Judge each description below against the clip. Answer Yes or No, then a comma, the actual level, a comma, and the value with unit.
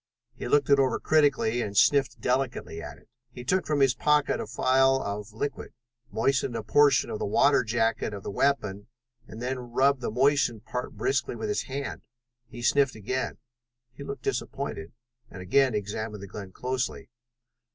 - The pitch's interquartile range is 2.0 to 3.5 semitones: No, average, 4.3 semitones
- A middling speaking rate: Yes, average, 170 wpm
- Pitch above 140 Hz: No, low, 125 Hz